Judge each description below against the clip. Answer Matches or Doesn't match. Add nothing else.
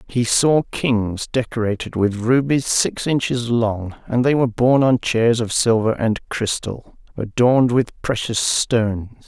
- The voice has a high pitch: Doesn't match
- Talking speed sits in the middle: Matches